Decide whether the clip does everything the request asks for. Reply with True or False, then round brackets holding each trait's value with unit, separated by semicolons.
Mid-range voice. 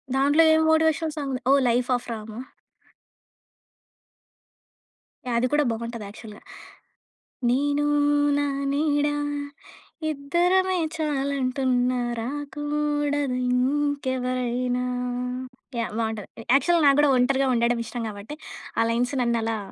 False (270 Hz)